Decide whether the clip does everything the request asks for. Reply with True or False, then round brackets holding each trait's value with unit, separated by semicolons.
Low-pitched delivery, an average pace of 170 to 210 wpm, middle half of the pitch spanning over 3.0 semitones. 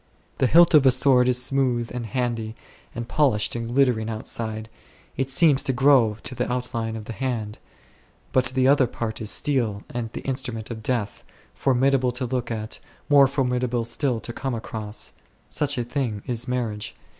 False (125 Hz; 180 wpm; 2.7 semitones)